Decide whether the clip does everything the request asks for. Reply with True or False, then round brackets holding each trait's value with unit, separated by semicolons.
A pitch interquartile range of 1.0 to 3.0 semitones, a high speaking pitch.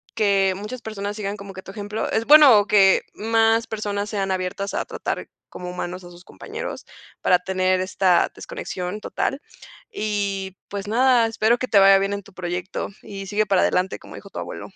True (2.5 semitones; 200 Hz)